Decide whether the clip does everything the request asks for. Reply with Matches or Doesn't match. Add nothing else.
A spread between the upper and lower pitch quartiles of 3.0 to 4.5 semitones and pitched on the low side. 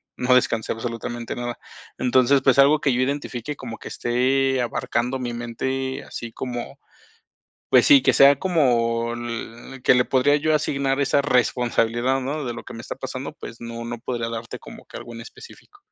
Doesn't match